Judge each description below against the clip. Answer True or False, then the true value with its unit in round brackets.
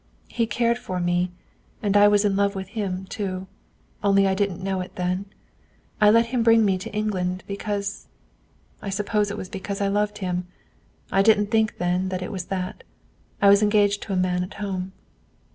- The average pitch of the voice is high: True (200 Hz)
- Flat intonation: True (2.0 semitones)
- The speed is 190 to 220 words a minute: True (195 wpm)